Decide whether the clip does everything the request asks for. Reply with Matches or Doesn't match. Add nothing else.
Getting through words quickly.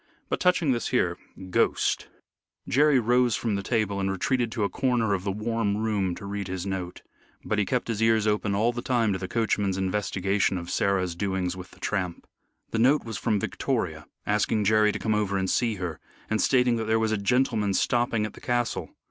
Matches